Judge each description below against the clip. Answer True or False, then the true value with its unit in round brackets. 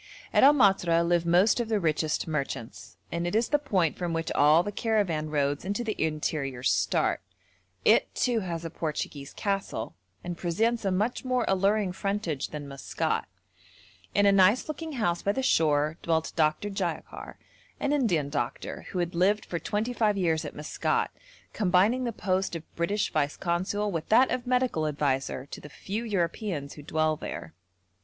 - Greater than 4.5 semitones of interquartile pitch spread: True (5.2 semitones)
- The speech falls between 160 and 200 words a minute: True (175 wpm)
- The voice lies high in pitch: False (180 Hz)